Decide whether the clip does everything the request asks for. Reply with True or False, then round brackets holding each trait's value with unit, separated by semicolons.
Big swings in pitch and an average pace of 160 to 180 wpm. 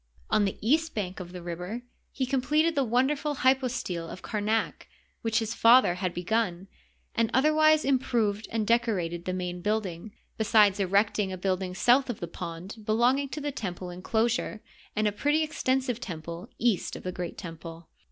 True (5.8 semitones; 170 wpm)